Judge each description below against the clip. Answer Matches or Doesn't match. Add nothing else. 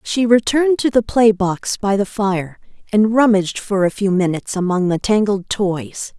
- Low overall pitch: Doesn't match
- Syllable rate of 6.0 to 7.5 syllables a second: Doesn't match